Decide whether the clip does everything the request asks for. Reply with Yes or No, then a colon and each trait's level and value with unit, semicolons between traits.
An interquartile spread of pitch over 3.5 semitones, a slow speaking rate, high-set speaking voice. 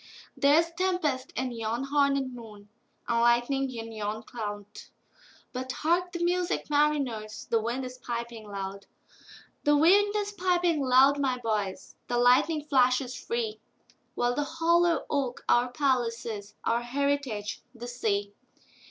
Yes: average, 4.3 semitones; slow, 115 wpm; very high, 250 Hz